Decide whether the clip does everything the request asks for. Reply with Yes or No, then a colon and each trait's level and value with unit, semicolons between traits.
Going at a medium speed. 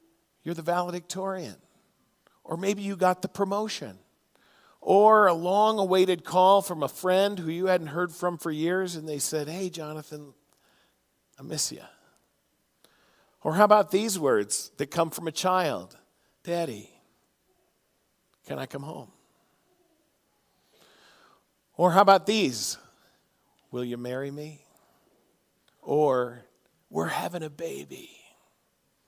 No: slow, 125 wpm